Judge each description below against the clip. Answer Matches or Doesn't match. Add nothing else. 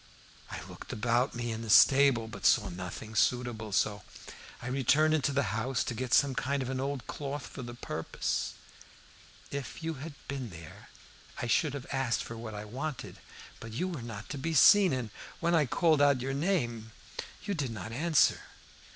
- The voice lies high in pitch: Doesn't match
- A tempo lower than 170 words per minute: Doesn't match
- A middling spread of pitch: Matches